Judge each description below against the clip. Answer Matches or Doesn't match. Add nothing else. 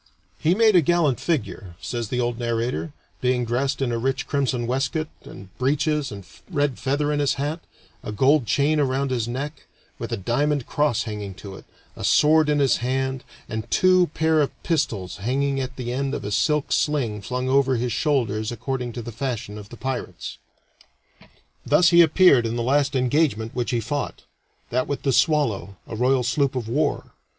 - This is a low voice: Matches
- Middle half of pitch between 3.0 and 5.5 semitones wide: Matches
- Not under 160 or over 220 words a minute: Matches